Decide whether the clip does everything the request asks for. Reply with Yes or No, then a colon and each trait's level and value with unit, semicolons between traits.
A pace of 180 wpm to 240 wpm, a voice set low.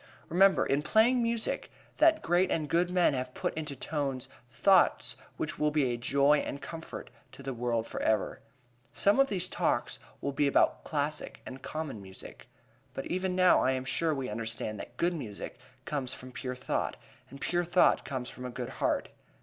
No: average, 185 wpm; medium, 145 Hz